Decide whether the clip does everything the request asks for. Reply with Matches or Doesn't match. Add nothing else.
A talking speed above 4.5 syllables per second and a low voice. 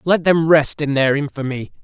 Doesn't match